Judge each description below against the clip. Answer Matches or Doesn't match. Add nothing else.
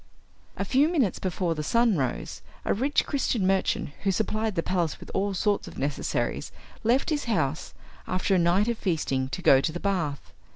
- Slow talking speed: Doesn't match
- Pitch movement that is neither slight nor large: Doesn't match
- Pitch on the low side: Doesn't match